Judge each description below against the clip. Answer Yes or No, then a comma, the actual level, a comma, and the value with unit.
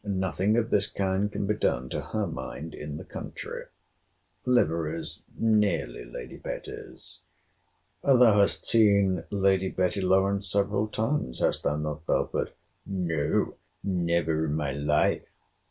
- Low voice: Yes, very low, 95 Hz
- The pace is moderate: No, slow, 125 wpm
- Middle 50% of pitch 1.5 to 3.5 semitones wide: No, average, 4.7 semitones